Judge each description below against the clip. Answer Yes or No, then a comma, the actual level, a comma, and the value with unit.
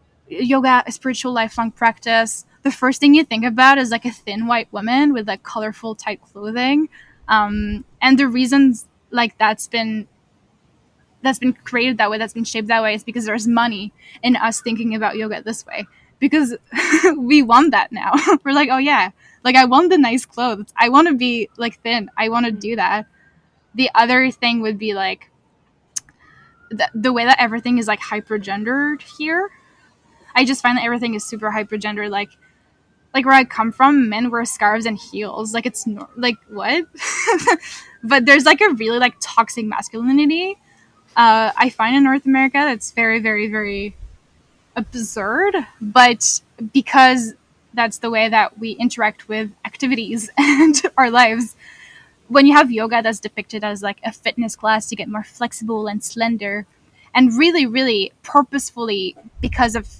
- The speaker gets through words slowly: No, average, 170 wpm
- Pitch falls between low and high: No, high, 235 Hz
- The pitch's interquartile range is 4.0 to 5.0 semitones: No, average, 3.4 semitones